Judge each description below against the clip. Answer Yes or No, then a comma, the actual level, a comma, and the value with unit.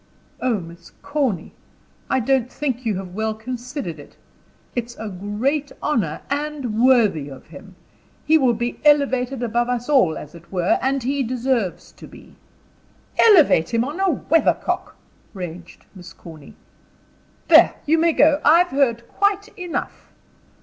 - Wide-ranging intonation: Yes, wide, 6.5 semitones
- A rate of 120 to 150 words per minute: Yes, average, 145 wpm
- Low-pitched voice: No, high, 245 Hz